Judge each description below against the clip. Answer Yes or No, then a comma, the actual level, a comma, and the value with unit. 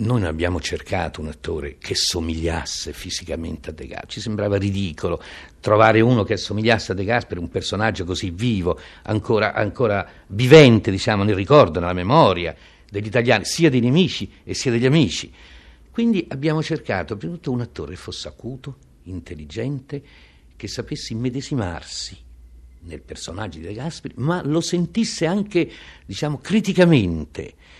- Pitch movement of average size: No, wide, 8.2 semitones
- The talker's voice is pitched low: Yes, low, 105 Hz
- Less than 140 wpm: No, average, 150 wpm